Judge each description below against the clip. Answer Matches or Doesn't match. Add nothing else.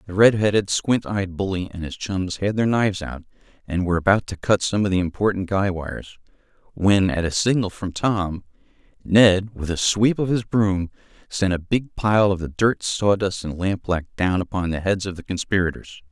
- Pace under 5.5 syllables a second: Matches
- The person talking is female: Doesn't match